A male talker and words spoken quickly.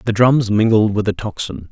Yes: male; fast, 210 wpm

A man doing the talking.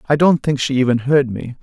Yes: male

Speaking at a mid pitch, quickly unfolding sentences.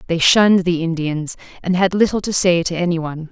Yes: medium, 175 Hz; fast, 215 wpm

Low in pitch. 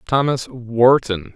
Yes: low, 120 Hz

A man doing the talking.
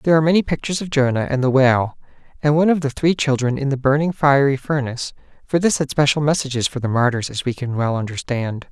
Yes: male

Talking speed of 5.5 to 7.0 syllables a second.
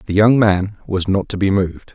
No: 5.0 syllables/s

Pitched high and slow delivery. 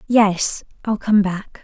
Yes: high, 205 Hz; slow, 110 wpm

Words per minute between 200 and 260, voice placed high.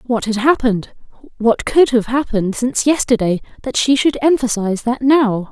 No: average, 150 wpm; high, 245 Hz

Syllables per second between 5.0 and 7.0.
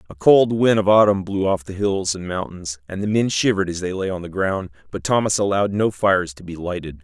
Yes: 5.8 syllables/s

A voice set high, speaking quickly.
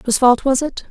Yes: very high, 255 Hz; fast, 265 wpm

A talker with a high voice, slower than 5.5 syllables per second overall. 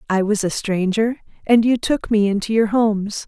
Yes: high, 215 Hz; 5.0 syllables/s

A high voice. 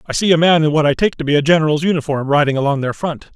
No: medium, 155 Hz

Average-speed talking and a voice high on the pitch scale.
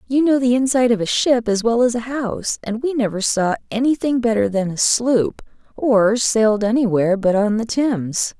No: fast, 215 wpm; high, 230 Hz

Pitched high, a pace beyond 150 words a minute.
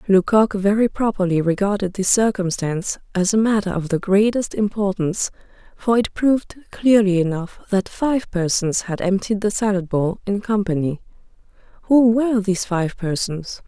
No: high, 200 Hz; average, 145 wpm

